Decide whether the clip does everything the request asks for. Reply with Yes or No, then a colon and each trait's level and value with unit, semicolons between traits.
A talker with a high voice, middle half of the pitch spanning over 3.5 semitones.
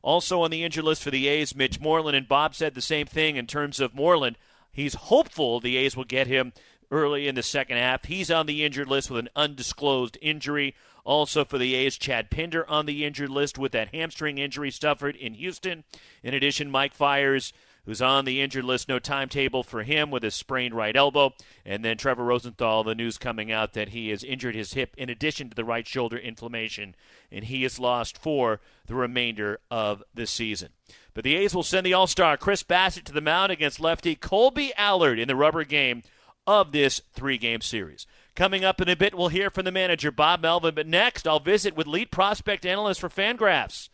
No: medium, 140 Hz; average, 4.4 semitones